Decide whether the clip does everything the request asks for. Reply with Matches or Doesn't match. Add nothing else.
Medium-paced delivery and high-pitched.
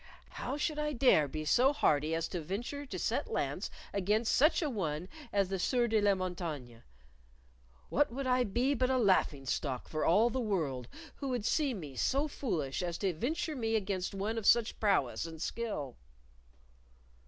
Matches